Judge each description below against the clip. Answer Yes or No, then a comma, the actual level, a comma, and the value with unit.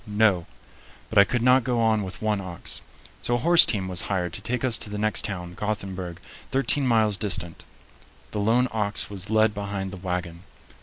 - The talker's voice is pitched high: No, low, 105 Hz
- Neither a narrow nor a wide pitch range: Yes, average, 3.1 semitones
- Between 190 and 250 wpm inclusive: Yes, average, 195 wpm